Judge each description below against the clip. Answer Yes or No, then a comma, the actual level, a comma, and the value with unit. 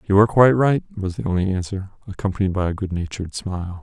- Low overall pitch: Yes, low, 100 Hz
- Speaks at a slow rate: No, fast, 205 wpm